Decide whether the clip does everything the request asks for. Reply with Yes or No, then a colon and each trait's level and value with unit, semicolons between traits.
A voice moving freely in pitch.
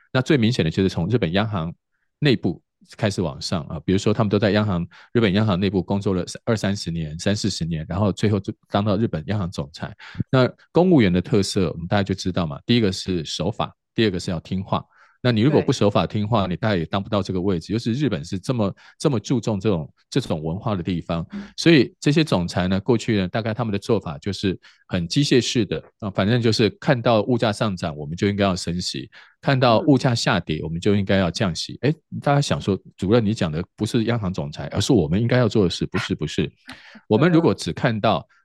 No: average, 4.1 semitones